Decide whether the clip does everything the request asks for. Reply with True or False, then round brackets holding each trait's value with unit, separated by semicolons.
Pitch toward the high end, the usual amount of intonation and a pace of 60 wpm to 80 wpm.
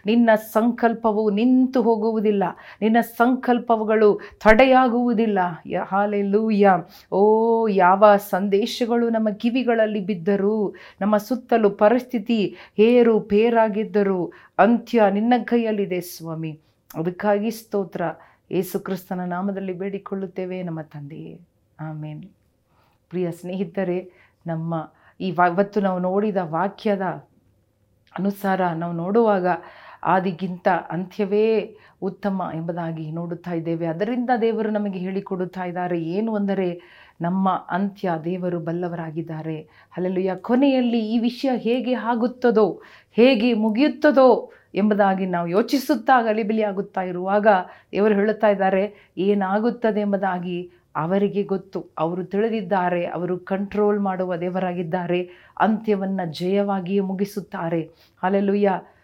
False (200 Hz; 3.4 semitones; 90 wpm)